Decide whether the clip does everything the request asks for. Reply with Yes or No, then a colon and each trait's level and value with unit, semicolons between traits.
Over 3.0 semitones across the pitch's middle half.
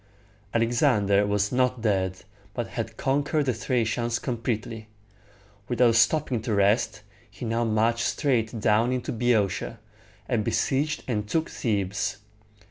No: average, 2.7 semitones